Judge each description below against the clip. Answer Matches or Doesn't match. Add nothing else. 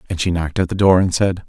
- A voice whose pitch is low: Matches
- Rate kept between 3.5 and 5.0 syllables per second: Doesn't match